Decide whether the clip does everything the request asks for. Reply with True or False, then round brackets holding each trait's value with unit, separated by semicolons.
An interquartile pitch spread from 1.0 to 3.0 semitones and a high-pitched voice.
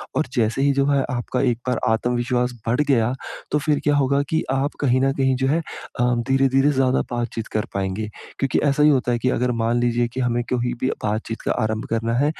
False (2.4 semitones; 125 Hz)